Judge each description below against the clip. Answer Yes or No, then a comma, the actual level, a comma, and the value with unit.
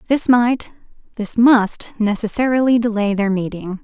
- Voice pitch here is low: No, high, 225 Hz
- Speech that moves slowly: Yes, slow, 125 wpm